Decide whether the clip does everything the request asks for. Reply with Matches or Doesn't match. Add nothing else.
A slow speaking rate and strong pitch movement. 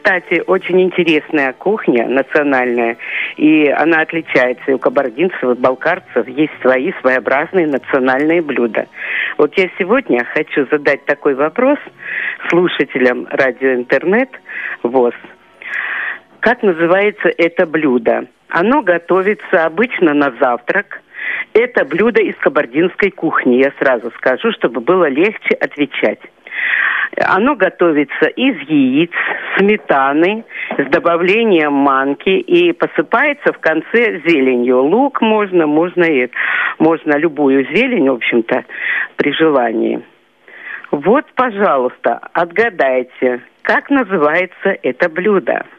Matches